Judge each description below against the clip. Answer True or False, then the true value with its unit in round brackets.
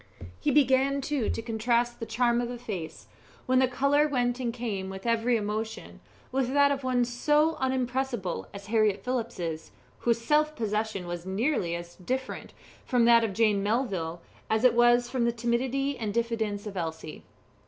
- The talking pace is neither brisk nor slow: True (170 wpm)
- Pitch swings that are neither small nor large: True (3.6 semitones)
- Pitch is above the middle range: True (235 Hz)